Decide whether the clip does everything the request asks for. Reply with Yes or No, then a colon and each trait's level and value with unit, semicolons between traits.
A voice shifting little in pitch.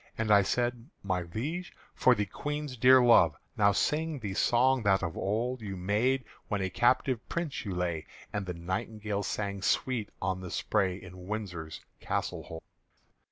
No: average, 5.0 semitones